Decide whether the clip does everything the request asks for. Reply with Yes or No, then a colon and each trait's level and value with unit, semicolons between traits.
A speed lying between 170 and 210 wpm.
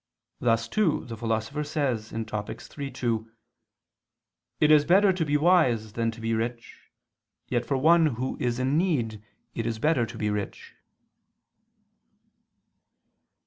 No: average, 140 wpm